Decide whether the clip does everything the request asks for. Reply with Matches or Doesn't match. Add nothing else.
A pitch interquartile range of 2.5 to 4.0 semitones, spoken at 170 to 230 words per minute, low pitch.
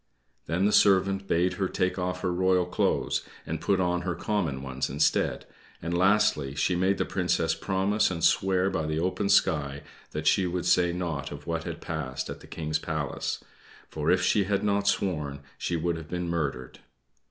Matches